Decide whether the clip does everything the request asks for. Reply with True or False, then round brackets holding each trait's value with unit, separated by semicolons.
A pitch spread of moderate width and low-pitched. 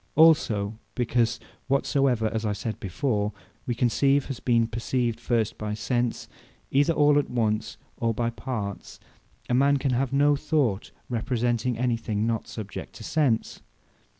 True (3.6 semitones; 120 Hz)